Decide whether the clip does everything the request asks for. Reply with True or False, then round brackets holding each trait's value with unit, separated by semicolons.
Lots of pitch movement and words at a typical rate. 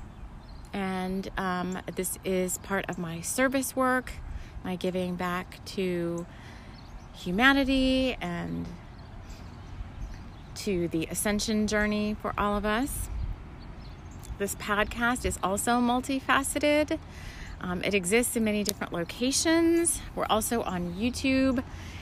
False (6.1 semitones; 105 wpm)